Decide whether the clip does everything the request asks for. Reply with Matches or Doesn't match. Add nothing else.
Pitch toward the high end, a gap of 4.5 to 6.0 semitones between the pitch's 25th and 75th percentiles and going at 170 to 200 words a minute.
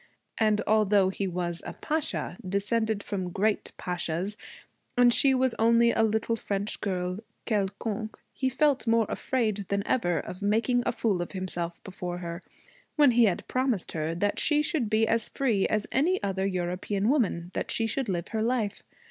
Doesn't match